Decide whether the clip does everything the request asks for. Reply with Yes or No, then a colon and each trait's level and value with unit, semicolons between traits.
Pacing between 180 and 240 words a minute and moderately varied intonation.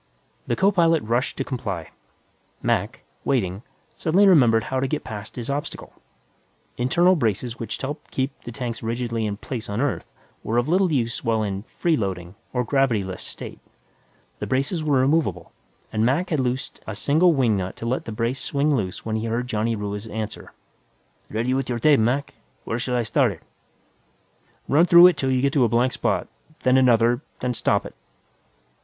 Yes: average, 185 wpm; average, 4.0 semitones